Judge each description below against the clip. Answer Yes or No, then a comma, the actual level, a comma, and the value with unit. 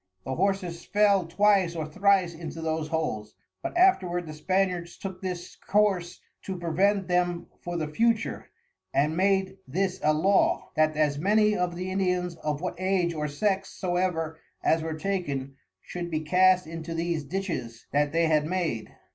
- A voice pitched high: No, medium, 175 Hz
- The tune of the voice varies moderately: Yes, average, 3.3 semitones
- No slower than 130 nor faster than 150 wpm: No, average, 165 wpm